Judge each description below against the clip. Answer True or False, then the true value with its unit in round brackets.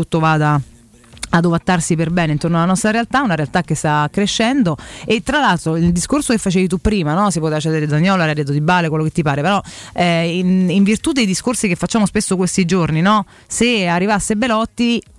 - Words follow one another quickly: True (205 wpm)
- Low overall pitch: False (180 Hz)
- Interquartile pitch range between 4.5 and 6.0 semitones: True (4.8 semitones)